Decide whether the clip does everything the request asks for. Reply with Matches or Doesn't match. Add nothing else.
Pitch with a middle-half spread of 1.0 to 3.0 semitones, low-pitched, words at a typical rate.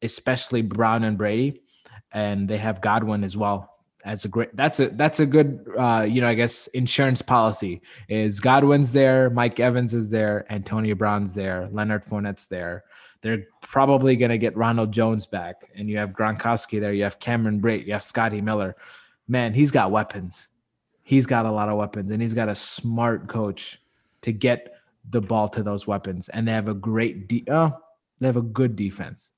Matches